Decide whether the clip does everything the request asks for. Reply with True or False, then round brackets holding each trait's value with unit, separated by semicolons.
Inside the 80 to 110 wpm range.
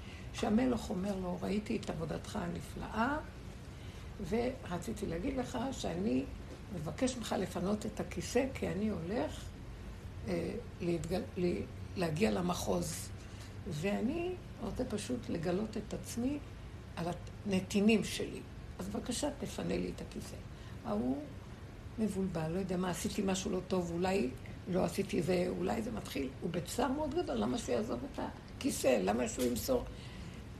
False (125 wpm)